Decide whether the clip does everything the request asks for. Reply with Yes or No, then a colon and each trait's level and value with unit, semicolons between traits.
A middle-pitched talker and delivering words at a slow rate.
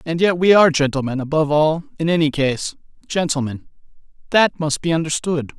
No: medium, 155 Hz; average, 160 wpm